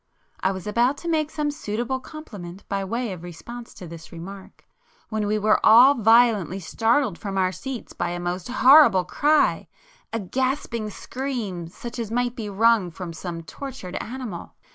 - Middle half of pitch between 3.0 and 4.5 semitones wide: No, average, 5.3 semitones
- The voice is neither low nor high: No, high, 220 Hz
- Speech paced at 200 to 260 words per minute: No, average, 165 wpm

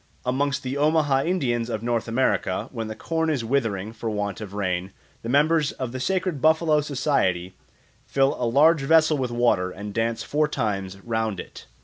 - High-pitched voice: No, low, 125 Hz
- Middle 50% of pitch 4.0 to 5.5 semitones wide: Yes, average, 5.2 semitones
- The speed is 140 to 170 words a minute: No, average, 180 wpm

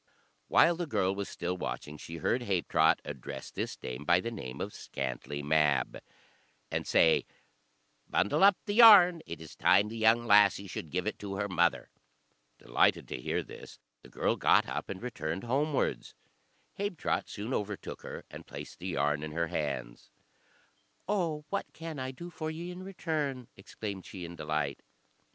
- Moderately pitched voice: No, low, 100 Hz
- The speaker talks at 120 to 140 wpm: No, average, 170 wpm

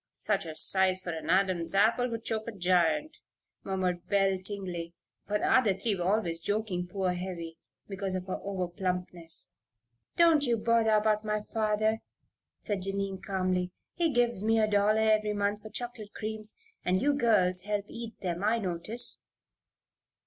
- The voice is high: Yes, high, 200 Hz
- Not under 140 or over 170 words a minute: Yes, average, 160 wpm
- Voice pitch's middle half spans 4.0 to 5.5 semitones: No, average, 3.1 semitones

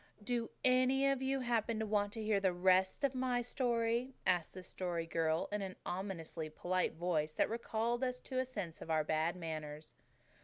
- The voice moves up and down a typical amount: No, wide, 6.2 semitones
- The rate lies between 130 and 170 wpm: No, average, 190 wpm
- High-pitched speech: Yes, high, 205 Hz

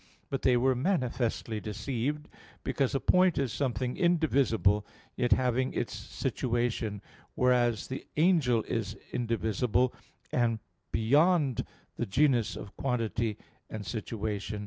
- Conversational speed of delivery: No, slow, 115 wpm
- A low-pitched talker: Yes, low, 120 Hz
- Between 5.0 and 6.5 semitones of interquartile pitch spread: No, average, 3.4 semitones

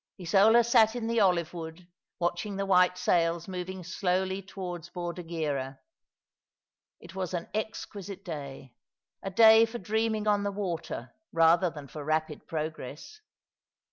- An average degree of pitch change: Yes, average, 3.5 semitones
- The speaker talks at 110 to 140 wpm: Yes, slow, 135 wpm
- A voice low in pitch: No, medium, 180 Hz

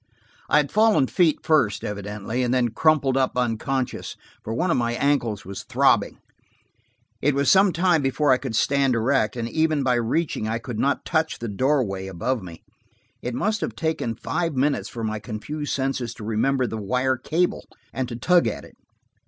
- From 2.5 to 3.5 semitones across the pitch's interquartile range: No, average, 4.6 semitones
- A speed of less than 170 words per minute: No, average, 185 wpm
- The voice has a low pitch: Yes, low, 130 Hz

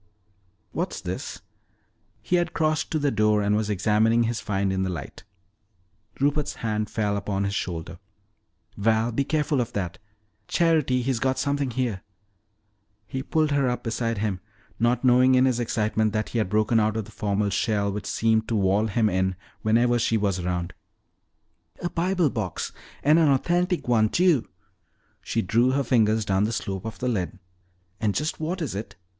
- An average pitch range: Yes, average, 4.1 semitones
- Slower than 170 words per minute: No, average, 175 wpm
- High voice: No, low, 115 Hz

